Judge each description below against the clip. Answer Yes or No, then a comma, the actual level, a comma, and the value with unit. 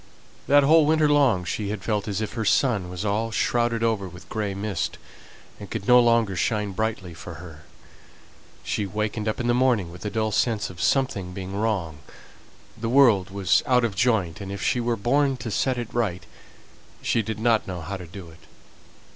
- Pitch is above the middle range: No, low, 105 Hz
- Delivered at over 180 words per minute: Yes, average, 195 wpm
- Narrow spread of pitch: No, average, 3.8 semitones